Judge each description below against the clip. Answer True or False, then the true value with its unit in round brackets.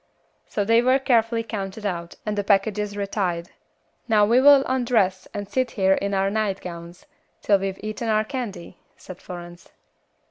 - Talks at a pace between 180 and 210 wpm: False (155 wpm)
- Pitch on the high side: True (205 Hz)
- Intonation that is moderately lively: True (3.1 semitones)